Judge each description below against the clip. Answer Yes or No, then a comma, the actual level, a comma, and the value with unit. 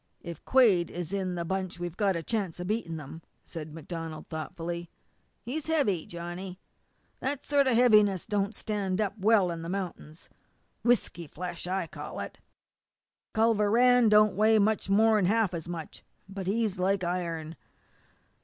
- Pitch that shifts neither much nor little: Yes, average, 4.0 semitones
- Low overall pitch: No, high, 190 Hz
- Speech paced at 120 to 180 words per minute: Yes, average, 160 wpm